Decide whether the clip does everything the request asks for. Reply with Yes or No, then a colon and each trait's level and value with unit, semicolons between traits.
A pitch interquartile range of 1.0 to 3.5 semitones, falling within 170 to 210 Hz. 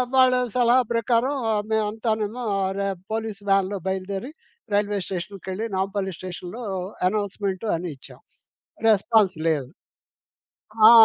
Yes: average, 2.7 semitones; high, 205 Hz